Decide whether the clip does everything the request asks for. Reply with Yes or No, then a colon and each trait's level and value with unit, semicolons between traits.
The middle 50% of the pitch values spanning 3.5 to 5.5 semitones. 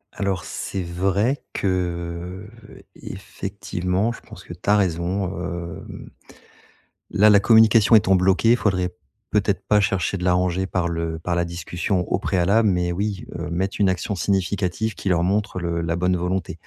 No: narrow, 2.5 semitones